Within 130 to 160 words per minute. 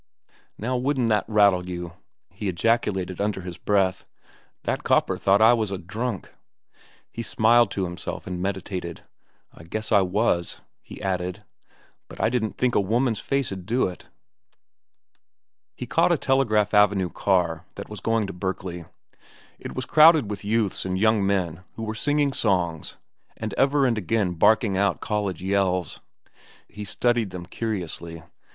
Yes: average, 150 wpm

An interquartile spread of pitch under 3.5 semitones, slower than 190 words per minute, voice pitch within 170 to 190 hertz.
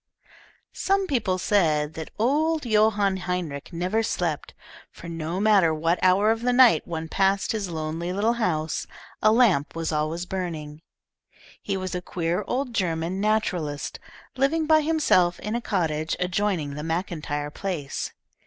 No: average, 5.0 semitones; average, 145 wpm; medium, 185 Hz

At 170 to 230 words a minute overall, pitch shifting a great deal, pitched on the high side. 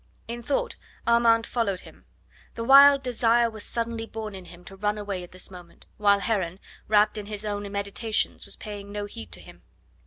No: average, 190 wpm; narrow, 2.5 semitones; high, 210 Hz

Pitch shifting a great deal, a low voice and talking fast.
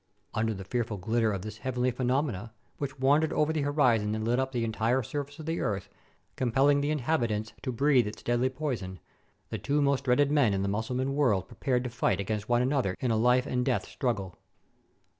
No: average, 4.1 semitones; low, 125 Hz; fast, 210 wpm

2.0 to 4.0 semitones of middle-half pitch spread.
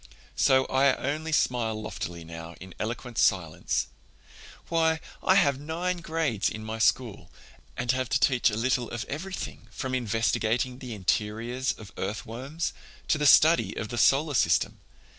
No: average, 4.7 semitones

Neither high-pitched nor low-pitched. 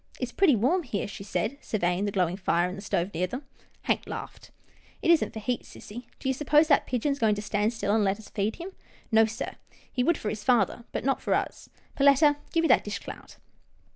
No: high, 225 Hz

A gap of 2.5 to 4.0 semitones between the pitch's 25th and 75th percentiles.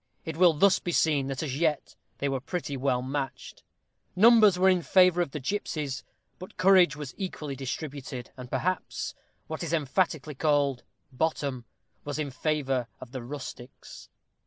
No: average, 4.6 semitones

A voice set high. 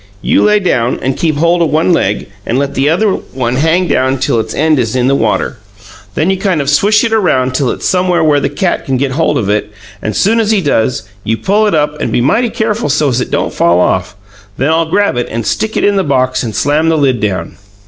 No: medium, 145 Hz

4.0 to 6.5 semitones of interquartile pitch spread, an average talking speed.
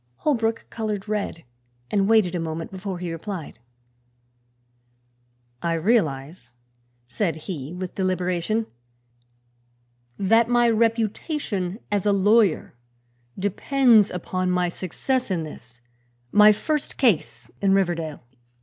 No: average, 4.3 semitones; slow, 105 wpm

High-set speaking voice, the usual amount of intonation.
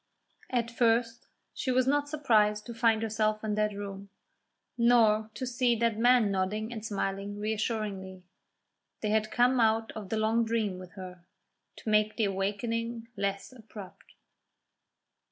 No: high, 220 Hz; narrow, 2.3 semitones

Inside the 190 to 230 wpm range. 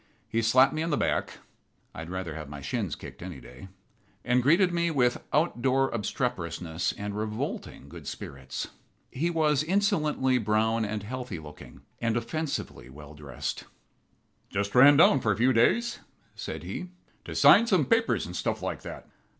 No: average, 165 wpm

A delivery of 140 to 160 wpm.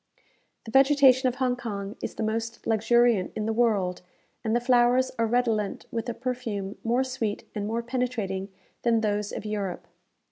No: average, 170 wpm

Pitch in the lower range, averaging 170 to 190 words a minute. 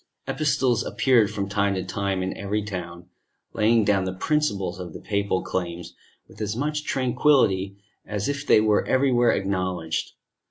No: low, 100 Hz; average, 155 wpm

